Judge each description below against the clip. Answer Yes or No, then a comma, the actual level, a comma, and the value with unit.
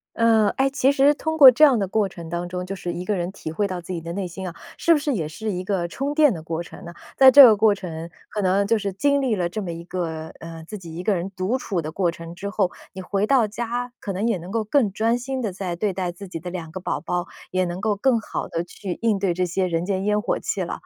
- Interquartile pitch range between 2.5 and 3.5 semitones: No, average, 4.3 semitones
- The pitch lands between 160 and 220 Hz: Yes, high, 195 Hz